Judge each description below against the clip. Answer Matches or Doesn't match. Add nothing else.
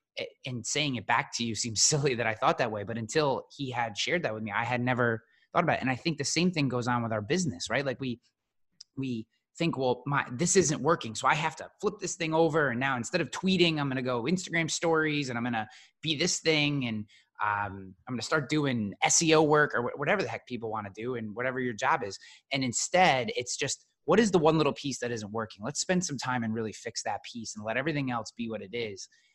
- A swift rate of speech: Matches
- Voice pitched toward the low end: Matches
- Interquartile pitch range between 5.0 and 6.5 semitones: Matches